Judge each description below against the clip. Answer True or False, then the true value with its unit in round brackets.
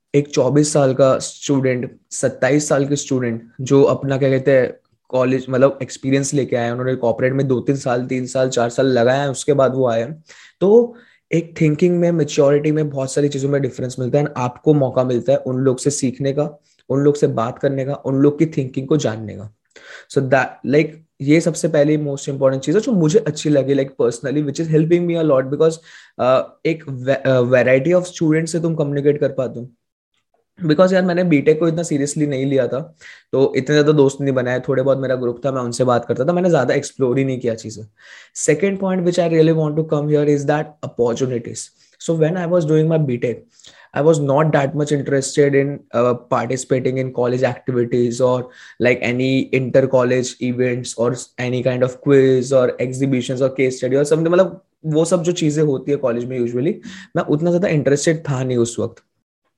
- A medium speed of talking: True (175 wpm)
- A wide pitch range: False (3.2 semitones)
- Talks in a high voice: False (135 Hz)